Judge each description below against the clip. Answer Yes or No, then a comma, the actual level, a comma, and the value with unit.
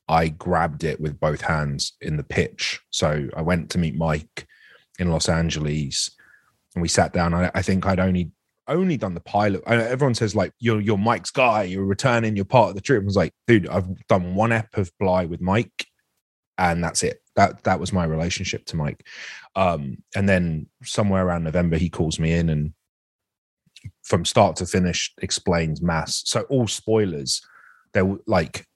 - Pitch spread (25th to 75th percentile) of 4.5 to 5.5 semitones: No, average, 4.0 semitones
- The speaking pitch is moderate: No, very low, 90 Hz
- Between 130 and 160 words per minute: No, average, 190 wpm